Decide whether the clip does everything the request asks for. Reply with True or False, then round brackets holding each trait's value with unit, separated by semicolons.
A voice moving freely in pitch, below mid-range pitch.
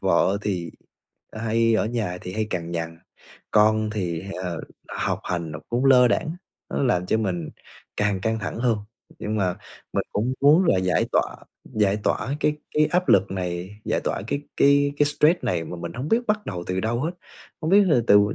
True (6.7 semitones; 110 Hz)